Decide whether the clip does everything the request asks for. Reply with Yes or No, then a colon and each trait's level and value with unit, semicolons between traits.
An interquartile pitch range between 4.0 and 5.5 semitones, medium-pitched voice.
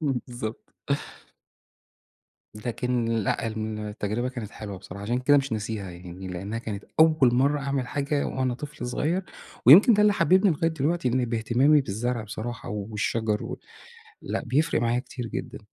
No: average, 4.4 semitones; low, 120 Hz